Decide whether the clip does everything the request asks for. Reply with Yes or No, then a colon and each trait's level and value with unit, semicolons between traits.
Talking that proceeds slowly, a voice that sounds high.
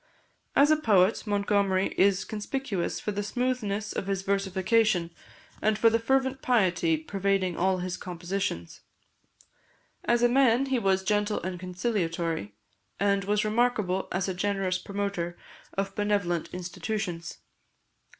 Yes: slow, 130 wpm; high, 200 Hz